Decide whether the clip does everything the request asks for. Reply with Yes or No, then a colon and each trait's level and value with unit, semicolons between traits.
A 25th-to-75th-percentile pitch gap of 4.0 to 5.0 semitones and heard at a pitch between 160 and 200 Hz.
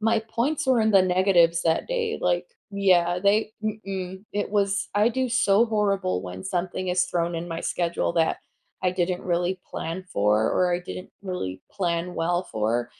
No: average, 3.3 semitones; medium, 185 Hz